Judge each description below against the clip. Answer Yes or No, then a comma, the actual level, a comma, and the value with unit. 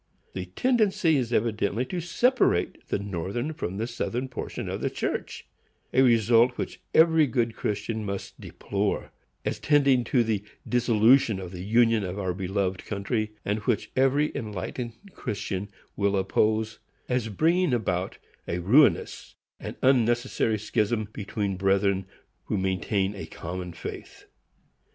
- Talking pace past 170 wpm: No, slow, 135 wpm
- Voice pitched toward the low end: Yes, low, 110 Hz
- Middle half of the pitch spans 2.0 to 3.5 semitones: No, average, 4.2 semitones